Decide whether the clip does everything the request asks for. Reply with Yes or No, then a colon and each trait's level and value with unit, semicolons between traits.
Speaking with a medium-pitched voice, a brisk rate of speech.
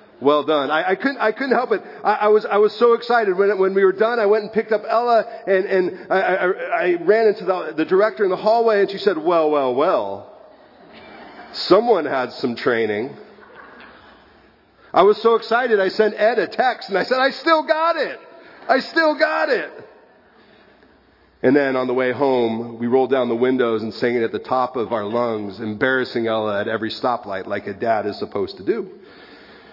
No: high, 195 Hz; fast, 210 wpm